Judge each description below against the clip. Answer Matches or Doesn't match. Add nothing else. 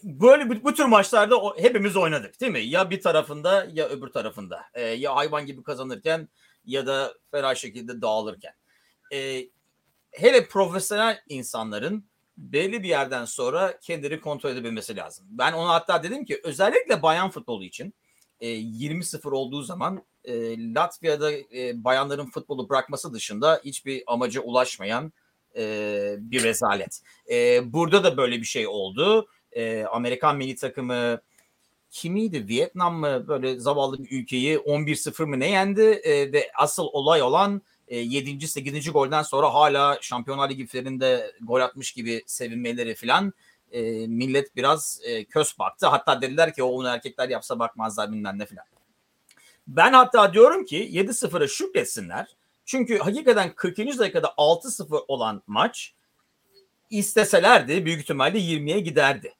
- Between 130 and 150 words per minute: Matches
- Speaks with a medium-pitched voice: Matches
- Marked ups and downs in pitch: Matches